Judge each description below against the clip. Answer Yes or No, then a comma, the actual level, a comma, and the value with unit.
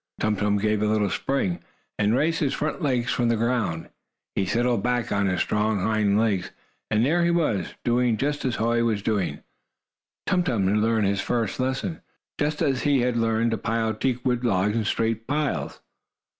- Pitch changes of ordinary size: Yes, average, 3.3 semitones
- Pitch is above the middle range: No, low, 115 Hz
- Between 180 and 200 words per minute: Yes, average, 185 wpm